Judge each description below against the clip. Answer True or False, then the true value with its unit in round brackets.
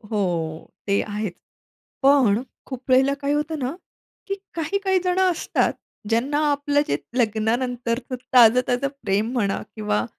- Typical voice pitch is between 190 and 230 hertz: False (255 Hz)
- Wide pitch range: False (4.5 semitones)